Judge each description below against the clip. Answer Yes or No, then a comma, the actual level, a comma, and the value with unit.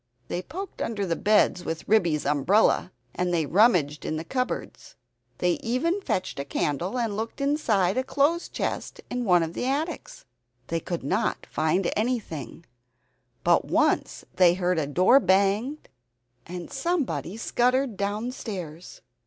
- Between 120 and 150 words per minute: Yes, average, 140 wpm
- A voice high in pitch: Yes, high, 195 Hz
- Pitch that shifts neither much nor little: No, wide, 6.5 semitones